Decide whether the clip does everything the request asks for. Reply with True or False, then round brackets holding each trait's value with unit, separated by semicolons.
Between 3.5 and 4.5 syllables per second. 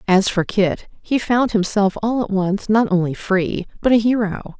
True (4.4 syllables/s)